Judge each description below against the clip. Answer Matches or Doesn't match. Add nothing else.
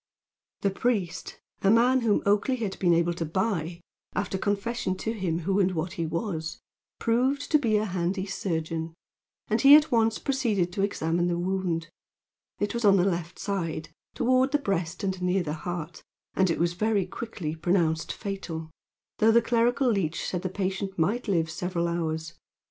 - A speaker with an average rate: Matches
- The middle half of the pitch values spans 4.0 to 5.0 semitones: Matches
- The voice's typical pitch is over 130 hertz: Matches